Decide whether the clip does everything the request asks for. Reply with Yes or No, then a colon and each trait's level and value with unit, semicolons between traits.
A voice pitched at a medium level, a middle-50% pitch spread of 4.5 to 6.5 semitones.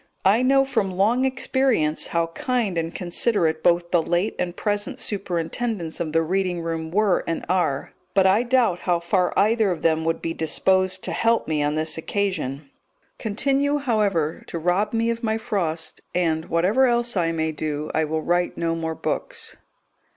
Yes: medium, 180 Hz; average, 5.0 semitones